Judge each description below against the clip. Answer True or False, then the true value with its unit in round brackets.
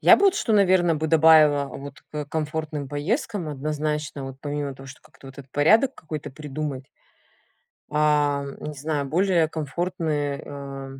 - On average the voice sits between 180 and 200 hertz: False (150 Hz)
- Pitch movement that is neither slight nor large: False (2.2 semitones)